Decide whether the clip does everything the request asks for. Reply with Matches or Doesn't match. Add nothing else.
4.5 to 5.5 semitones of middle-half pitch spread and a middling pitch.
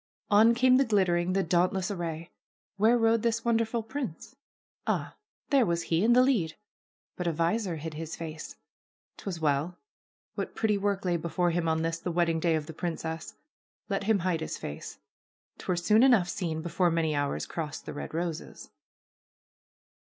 Matches